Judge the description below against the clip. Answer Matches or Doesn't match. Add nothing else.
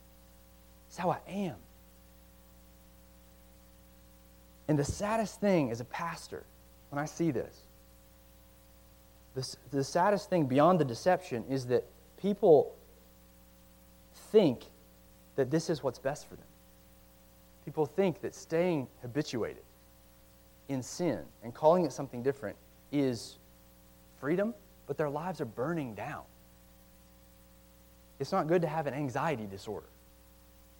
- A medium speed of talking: Doesn't match